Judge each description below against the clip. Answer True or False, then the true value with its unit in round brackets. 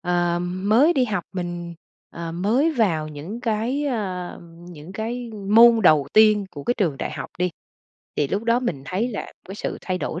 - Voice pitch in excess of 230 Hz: False (195 Hz)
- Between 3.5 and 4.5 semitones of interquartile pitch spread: False (5.0 semitones)